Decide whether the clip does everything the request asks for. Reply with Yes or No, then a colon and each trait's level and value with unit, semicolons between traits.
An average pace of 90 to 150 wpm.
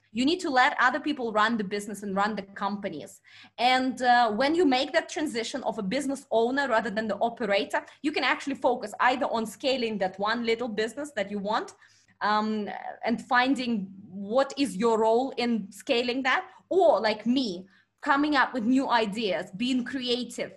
No: average, 180 wpm